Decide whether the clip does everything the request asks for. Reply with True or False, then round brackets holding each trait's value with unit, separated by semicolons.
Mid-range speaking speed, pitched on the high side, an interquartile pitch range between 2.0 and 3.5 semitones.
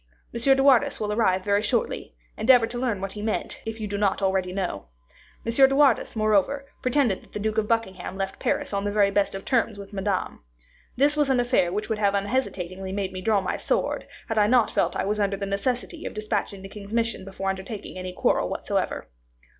False (220 wpm; 210 Hz; 3.1 semitones)